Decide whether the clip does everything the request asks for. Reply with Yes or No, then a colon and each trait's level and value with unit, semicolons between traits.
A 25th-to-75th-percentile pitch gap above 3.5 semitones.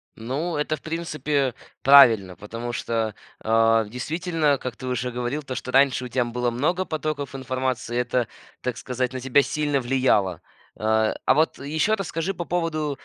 Yes: average, 4.0 semitones